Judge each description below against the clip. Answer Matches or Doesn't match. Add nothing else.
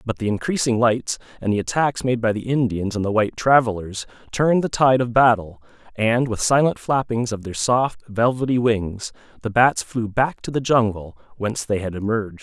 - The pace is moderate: Matches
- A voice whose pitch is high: Doesn't match